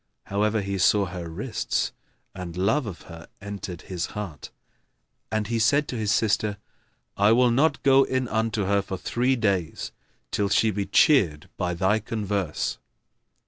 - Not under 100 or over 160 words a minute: Yes, average, 155 wpm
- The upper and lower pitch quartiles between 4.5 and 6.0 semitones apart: No, average, 3.1 semitones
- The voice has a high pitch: No, low, 105 Hz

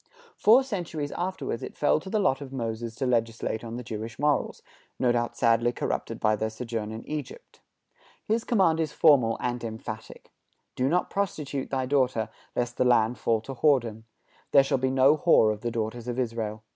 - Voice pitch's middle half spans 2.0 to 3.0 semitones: No, average, 4.3 semitones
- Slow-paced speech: No, average, 185 wpm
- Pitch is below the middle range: Yes, low, 125 Hz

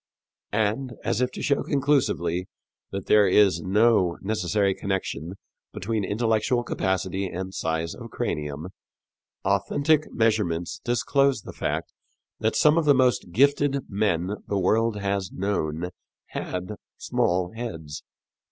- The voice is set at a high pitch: No, low, 100 Hz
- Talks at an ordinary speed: No, slow, 125 wpm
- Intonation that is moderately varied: Yes, average, 4.7 semitones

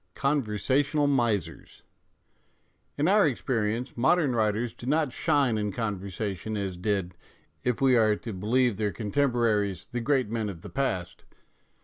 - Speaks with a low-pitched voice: Yes, low, 115 Hz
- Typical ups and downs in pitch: Yes, average, 4.5 semitones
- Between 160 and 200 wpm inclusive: No, average, 145 wpm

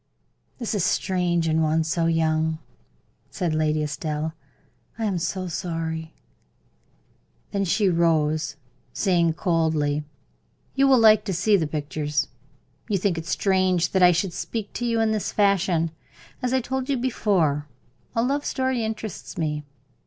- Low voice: No, medium, 175 Hz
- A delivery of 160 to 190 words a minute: No, average, 145 wpm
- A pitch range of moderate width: Yes, average, 4.8 semitones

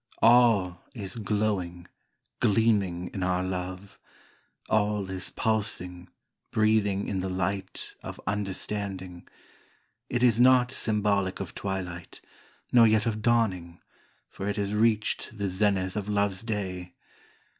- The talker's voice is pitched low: Yes, low, 100 Hz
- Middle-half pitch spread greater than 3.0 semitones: No, average, 2.7 semitones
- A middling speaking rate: No, slow, 125 wpm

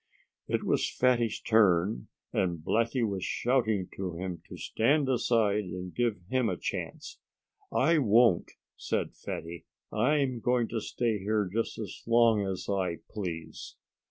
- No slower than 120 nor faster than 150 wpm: Yes, average, 140 wpm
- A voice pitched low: Yes, low, 110 Hz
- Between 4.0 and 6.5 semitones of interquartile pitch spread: Yes, average, 4.3 semitones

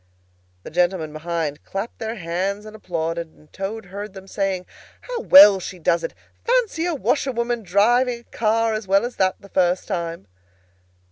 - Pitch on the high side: Yes, high, 195 Hz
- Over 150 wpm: Yes, average, 165 wpm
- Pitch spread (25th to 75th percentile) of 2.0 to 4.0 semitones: No, average, 4.5 semitones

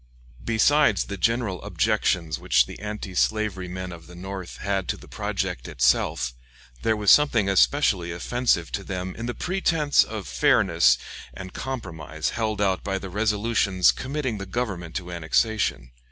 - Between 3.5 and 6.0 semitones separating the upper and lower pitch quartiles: Yes, average, 4.2 semitones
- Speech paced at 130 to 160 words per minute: Yes, average, 155 wpm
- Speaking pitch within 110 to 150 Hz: No, low, 100 Hz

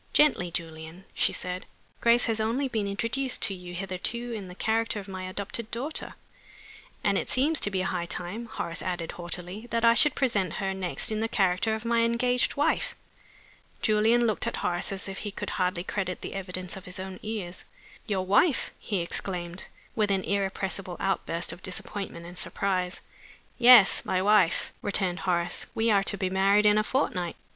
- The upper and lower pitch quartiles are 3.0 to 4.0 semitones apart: Yes, average, 3.6 semitones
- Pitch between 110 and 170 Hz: No, high, 195 Hz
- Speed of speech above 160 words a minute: Yes, average, 185 wpm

